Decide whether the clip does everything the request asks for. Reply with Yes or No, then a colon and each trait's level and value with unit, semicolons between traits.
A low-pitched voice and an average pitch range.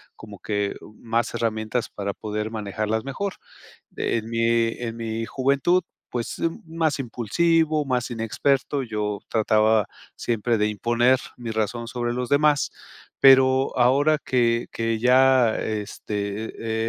Yes: low, 115 Hz; average, 3.1 semitones